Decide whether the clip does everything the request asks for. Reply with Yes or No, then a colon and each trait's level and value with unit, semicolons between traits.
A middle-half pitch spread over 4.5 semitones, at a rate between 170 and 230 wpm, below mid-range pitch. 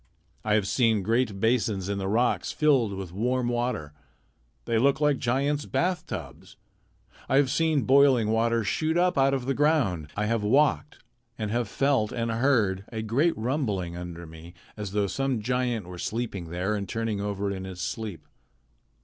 Yes: average, 5.1 semitones; average, 175 wpm; low, 115 Hz